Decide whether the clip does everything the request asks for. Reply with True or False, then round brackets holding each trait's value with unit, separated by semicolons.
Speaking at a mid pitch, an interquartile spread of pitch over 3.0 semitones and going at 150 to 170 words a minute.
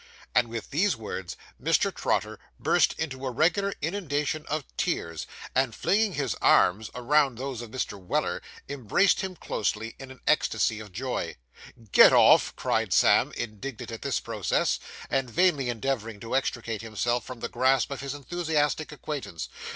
False (130 Hz; 4.5 semitones; 155 wpm)